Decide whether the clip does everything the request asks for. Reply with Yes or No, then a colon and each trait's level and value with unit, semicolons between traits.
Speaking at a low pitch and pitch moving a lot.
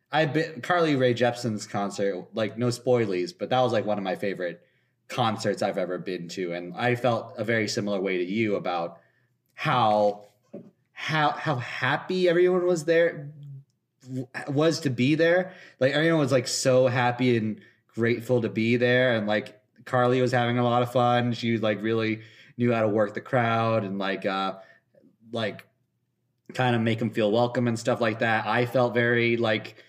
No: low, 120 Hz; average, 2.9 semitones